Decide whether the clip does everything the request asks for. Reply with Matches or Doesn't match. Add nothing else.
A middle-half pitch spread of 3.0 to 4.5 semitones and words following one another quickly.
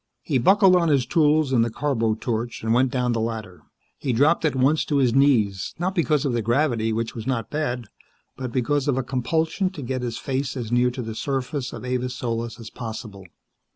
Matches